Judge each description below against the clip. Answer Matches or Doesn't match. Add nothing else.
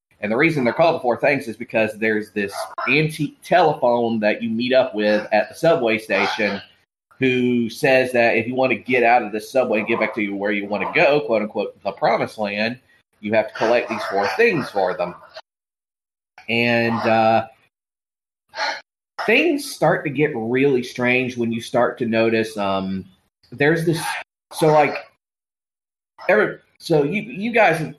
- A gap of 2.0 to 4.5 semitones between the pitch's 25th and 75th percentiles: Matches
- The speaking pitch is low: Matches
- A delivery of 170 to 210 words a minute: Matches